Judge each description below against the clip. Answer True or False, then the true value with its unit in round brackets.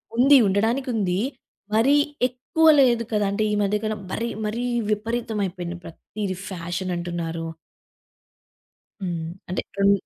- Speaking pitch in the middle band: False (205 Hz)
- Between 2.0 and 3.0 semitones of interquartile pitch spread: False (4.5 semitones)